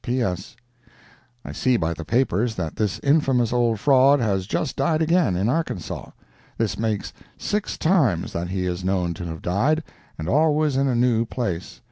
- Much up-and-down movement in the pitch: Yes, wide, 6.9 semitones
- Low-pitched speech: Yes, low, 115 Hz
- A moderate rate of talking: Yes, average, 170 wpm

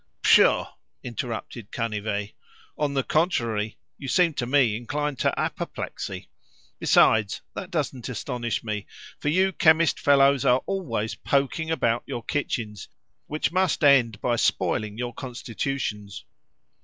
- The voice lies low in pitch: Yes, low, 125 Hz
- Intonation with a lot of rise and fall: No, average, 4.7 semitones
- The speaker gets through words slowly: Yes, slow, 125 wpm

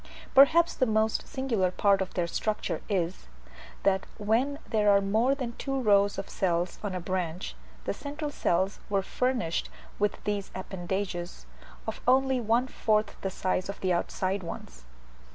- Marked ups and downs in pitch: No, average, 4.2 semitones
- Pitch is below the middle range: No, high, 200 Hz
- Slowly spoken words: No, average, 155 wpm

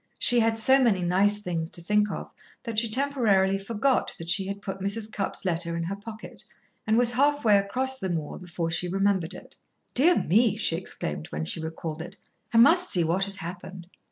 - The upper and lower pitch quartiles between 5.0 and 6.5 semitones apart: No, average, 4.6 semitones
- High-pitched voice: Yes, high, 200 Hz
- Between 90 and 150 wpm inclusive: No, fast, 205 wpm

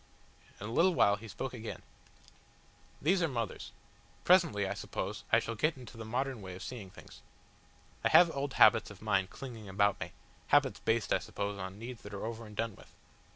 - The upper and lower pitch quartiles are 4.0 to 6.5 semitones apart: Yes, average, 4.3 semitones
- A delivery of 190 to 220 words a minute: Yes, average, 200 wpm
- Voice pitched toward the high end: No, low, 110 Hz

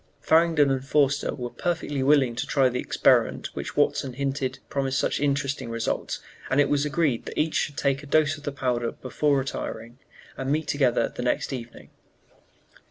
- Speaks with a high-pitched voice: No, medium, 140 Hz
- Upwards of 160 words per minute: Yes, average, 175 wpm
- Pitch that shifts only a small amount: Yes, narrow, 2.3 semitones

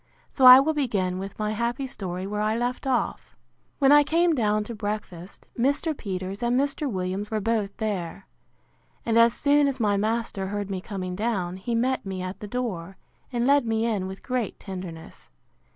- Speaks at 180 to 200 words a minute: Yes, average, 185 wpm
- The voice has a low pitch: No, high, 215 Hz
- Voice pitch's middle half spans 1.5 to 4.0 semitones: No, average, 4.5 semitones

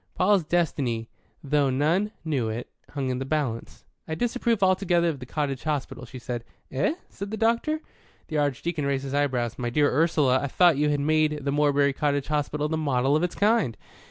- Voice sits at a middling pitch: Yes, medium, 145 Hz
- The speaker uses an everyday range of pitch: Yes, average, 4.0 semitones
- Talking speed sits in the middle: Yes, average, 190 wpm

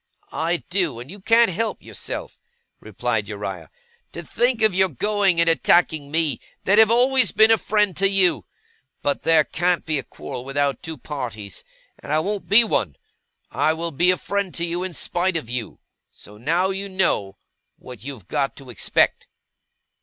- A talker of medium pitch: Yes, medium, 170 Hz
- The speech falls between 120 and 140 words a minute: No, average, 175 wpm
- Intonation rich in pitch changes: Yes, wide, 5.8 semitones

